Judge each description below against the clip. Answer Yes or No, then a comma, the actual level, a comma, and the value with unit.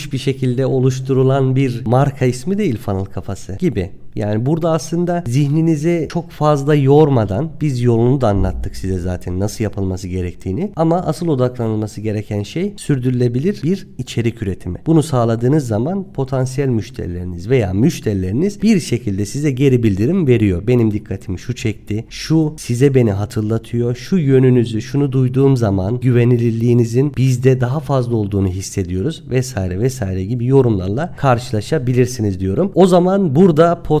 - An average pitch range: No, wide, 5.7 semitones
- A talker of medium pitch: No, low, 125 Hz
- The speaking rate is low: No, average, 135 wpm